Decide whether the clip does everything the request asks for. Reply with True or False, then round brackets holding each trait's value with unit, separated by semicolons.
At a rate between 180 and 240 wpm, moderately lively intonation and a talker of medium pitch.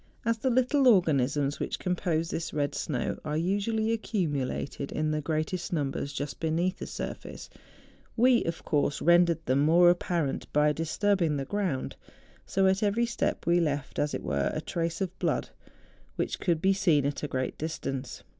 False (170 wpm; 4.6 semitones; 165 Hz)